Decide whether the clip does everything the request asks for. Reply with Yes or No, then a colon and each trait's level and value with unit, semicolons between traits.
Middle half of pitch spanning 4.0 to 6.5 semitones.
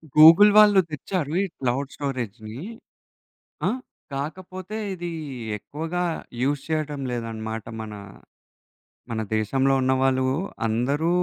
Yes: wide, 5.4 semitones